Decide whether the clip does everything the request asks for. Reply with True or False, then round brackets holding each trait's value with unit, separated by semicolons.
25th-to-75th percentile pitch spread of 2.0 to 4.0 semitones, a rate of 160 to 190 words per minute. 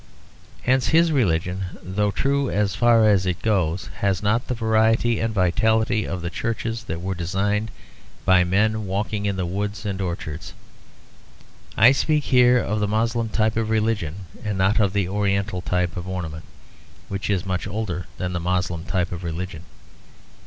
True (3.5 semitones; 165 wpm)